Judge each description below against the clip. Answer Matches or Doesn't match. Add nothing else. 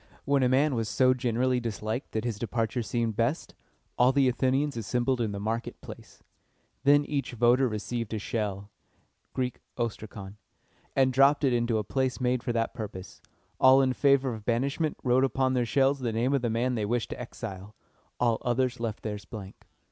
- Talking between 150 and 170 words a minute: Doesn't match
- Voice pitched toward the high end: Doesn't match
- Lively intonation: Doesn't match